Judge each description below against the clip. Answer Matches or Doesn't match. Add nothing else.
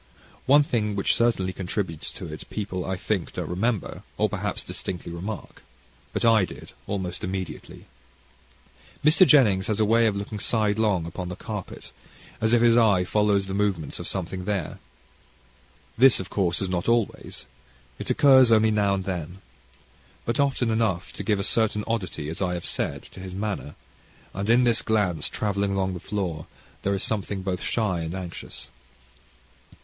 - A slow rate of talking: Doesn't match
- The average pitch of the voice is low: Matches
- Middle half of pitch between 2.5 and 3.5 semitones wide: Matches